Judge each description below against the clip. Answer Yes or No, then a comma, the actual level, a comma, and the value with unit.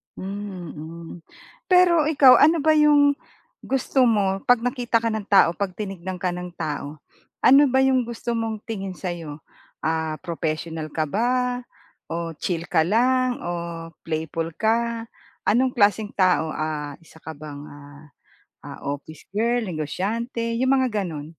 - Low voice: No, high, 195 Hz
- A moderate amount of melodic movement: No, wide, 7.1 semitones